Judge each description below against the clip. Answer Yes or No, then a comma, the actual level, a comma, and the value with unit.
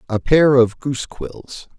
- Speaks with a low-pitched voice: Yes, low, 130 Hz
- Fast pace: No, average, 170 wpm